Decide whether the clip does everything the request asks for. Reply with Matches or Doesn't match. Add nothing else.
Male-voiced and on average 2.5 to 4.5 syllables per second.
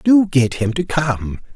Matches